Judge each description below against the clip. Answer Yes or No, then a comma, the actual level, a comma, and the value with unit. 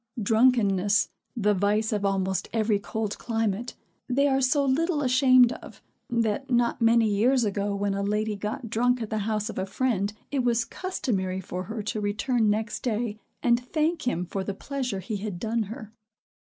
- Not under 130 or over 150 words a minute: No, average, 180 wpm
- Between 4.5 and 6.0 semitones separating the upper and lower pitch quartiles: No, average, 3.4 semitones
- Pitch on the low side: No, high, 220 Hz